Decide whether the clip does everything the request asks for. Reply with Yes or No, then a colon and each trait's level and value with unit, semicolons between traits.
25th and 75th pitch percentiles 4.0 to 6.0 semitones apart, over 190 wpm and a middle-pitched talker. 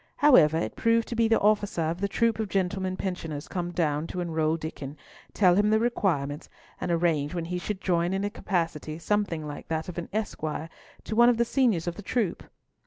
Yes: average, 4.4 semitones; fast, 205 wpm; medium, 180 Hz